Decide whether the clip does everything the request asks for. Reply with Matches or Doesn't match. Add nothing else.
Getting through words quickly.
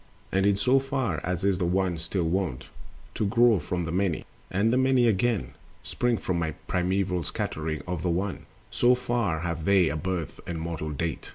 Doesn't match